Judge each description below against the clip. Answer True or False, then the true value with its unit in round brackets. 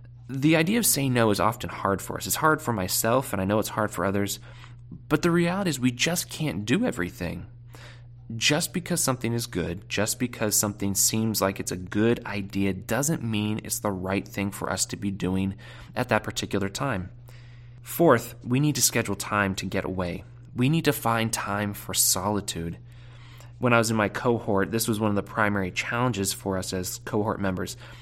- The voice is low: True (115 Hz)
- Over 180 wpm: True (200 wpm)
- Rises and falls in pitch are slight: False (3.6 semitones)